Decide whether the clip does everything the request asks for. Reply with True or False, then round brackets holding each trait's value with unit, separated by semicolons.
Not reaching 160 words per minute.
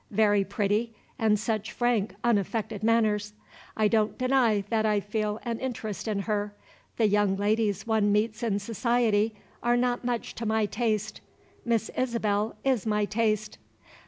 True (150 wpm)